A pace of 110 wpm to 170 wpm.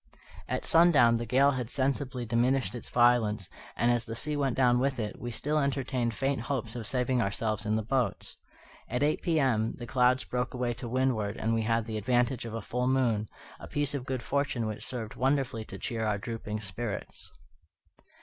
No: average, 195 wpm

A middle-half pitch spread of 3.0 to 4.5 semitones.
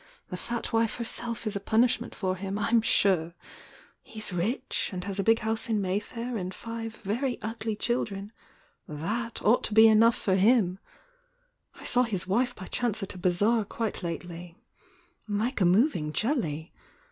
Yes: average, 3.7 semitones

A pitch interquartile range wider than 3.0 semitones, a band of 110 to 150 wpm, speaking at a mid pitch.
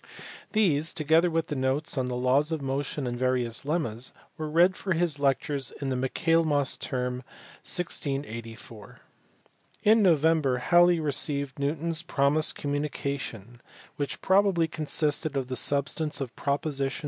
Yes: average, 3.6 semitones; slow, 135 wpm; medium, 145 Hz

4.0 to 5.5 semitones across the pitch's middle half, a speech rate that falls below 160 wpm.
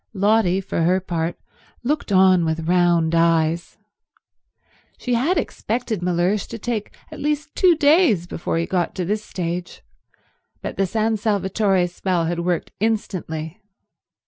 Yes: average, 4.3 semitones; average, 140 wpm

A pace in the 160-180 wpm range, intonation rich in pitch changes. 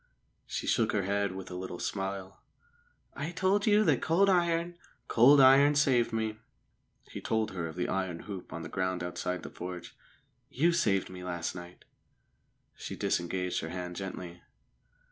Yes: average, 165 wpm; wide, 7.8 semitones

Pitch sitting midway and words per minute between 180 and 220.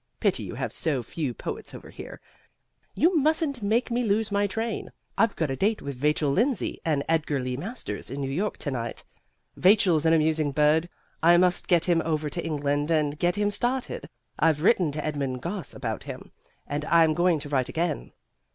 Yes: medium, 165 Hz; average, 190 wpm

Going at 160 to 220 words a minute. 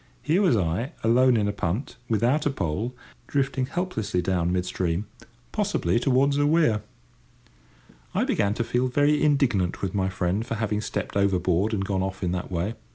Yes: average, 170 wpm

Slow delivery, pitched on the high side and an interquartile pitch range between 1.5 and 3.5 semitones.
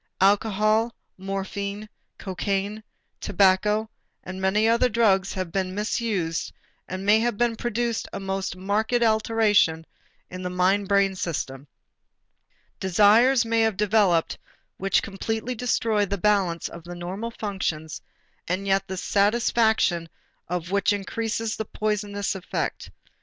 Yes: slow, 125 wpm; high, 200 Hz; average, 2.7 semitones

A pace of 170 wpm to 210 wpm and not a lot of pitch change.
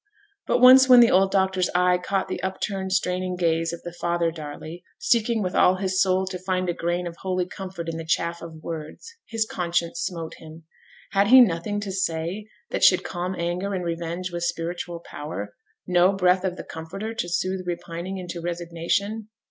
Yes: average, 190 wpm; narrow, 2.0 semitones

